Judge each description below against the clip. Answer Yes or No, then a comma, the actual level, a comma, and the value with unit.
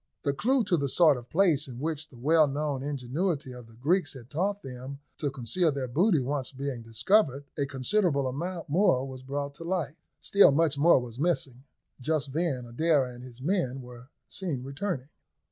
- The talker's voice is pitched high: No, medium, 140 Hz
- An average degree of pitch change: Yes, average, 4.4 semitones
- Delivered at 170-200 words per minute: Yes, average, 180 wpm